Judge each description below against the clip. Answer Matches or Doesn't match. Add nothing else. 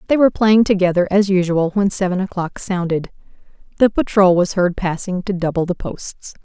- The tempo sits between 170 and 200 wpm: Matches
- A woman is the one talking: Matches